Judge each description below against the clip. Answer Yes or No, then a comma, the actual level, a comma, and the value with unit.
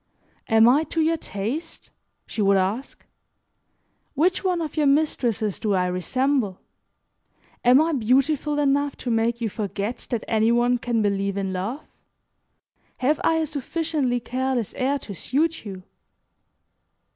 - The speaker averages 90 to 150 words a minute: Yes, average, 140 wpm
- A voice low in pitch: No, high, 245 Hz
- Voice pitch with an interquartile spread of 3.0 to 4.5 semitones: No, wide, 5.4 semitones